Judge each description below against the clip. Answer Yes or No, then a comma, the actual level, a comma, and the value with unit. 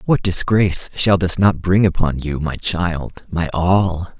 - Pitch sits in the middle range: No, very low, 90 Hz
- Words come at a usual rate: Yes, average, 170 wpm